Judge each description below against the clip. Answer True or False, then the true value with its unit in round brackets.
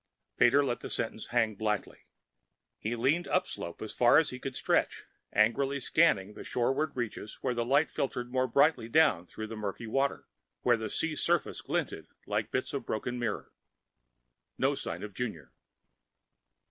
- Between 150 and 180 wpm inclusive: True (160 wpm)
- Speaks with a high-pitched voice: False (120 Hz)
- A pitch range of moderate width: True (3.8 semitones)